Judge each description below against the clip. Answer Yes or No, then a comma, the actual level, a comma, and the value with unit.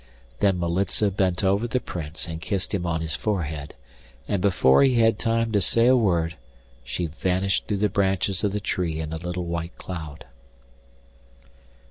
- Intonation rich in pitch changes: No, average, 3.5 semitones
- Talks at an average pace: Yes, average, 170 wpm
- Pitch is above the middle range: No, very low, 90 Hz